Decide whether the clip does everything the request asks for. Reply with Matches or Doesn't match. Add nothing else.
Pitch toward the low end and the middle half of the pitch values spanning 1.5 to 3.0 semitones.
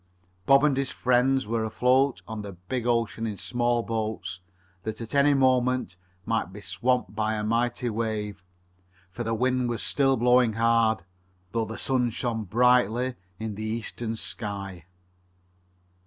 Matches